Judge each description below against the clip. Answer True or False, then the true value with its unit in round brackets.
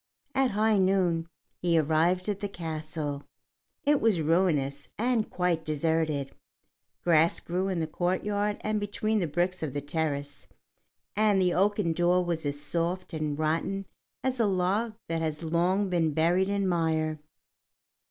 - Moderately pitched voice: True (175 Hz)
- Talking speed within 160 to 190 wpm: False (150 wpm)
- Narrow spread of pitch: False (3.7 semitones)